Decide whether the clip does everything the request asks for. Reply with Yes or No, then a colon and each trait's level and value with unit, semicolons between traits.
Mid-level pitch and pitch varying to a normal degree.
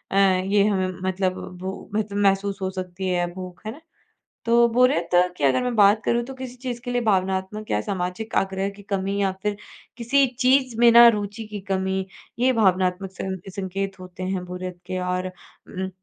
No: high, 195 Hz; average, 3.0 semitones